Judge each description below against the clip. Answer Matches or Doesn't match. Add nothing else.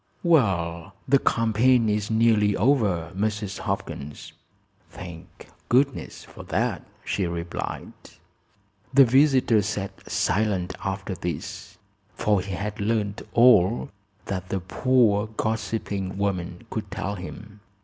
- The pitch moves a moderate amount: Matches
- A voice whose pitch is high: Doesn't match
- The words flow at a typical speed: Doesn't match